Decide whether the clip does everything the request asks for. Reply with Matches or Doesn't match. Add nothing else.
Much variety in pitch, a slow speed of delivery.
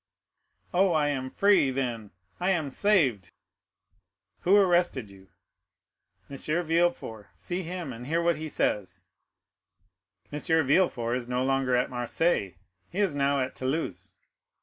Matches